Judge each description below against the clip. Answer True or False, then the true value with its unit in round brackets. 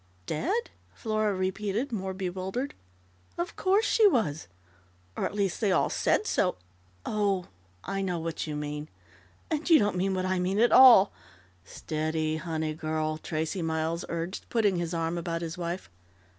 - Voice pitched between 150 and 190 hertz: True (185 Hz)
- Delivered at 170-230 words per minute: False (160 wpm)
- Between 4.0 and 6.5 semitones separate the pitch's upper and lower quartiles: True (4.6 semitones)